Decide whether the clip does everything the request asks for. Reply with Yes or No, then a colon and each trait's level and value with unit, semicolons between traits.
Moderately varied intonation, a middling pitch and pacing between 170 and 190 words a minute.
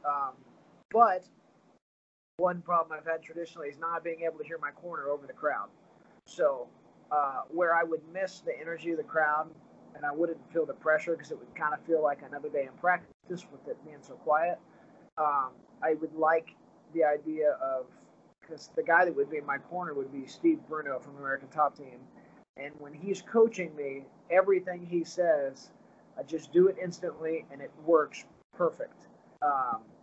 Yes: average, 3.4 semitones; medium, 165 Hz; average, 185 wpm